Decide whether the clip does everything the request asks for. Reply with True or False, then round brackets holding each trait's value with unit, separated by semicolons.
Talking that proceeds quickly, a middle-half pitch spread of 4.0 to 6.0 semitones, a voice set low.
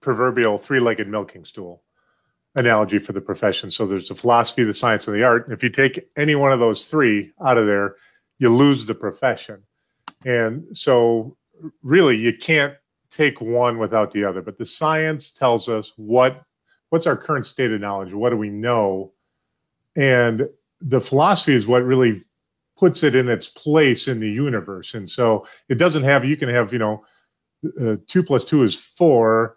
False (180 wpm; 4.5 semitones; 120 Hz)